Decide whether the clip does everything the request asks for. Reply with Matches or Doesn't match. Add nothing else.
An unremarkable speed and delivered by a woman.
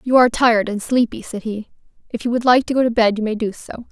Doesn't match